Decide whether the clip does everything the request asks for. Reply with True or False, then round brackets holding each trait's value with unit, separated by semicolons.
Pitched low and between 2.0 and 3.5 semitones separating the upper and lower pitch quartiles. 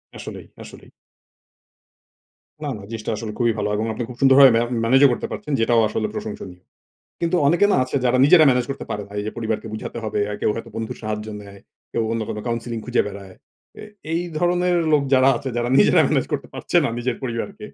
False (120 Hz; 3.9 semitones)